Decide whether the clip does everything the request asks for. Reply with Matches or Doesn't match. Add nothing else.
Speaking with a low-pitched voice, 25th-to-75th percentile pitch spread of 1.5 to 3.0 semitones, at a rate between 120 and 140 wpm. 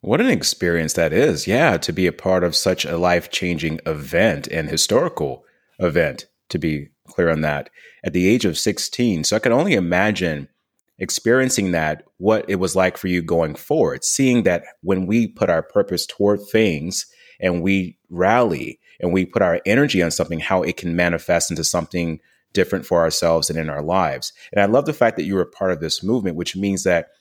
Doesn't match